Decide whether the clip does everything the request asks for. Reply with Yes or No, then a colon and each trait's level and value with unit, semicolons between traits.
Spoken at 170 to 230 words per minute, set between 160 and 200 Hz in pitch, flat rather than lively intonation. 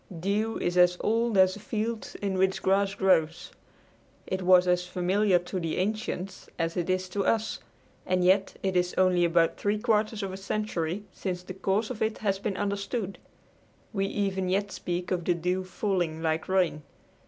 Yes: average, 180 wpm; high, 190 Hz; narrow, 2.3 semitones